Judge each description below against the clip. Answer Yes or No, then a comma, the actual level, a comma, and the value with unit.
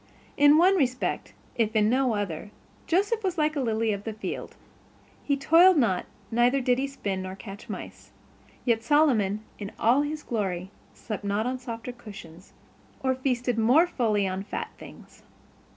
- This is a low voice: No, high, 240 Hz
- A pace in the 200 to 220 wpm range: No, average, 165 wpm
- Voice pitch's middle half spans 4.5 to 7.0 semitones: Yes, average, 5.1 semitones